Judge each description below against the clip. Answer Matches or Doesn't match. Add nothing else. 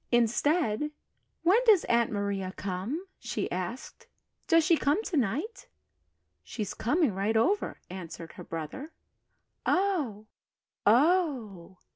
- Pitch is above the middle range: Matches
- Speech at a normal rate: Doesn't match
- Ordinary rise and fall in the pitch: Doesn't match